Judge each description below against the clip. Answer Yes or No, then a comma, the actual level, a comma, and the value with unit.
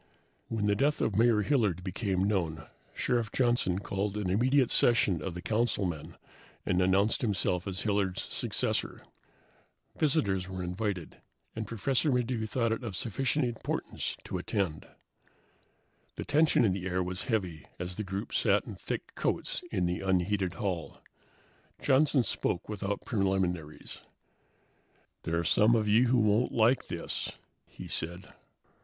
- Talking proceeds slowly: No, average, 145 wpm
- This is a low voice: Yes, low, 100 Hz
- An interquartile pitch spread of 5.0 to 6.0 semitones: No, average, 4.2 semitones